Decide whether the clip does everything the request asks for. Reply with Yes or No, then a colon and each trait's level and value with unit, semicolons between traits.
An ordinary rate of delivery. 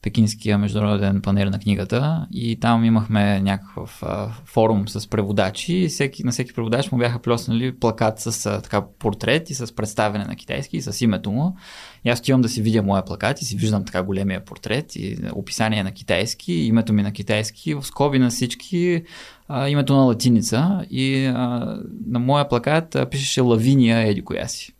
No: fast, 185 wpm